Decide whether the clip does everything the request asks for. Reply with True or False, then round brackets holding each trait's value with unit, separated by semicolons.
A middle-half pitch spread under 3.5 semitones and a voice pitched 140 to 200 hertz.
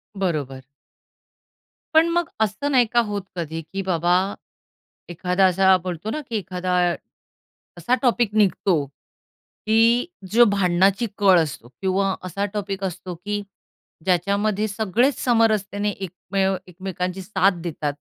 True (2.7 semitones; 195 Hz)